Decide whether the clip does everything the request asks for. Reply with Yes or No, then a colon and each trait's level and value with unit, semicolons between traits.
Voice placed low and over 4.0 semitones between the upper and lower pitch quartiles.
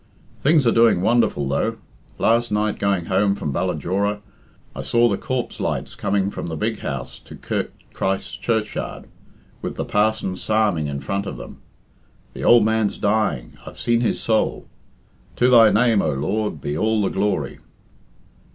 No: low, 105 Hz; average, 3.3 semitones